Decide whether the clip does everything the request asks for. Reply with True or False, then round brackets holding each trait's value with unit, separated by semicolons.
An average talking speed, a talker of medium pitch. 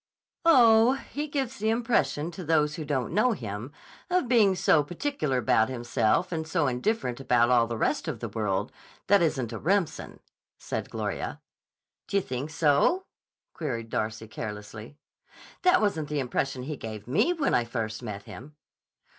True (160 wpm; 150 Hz)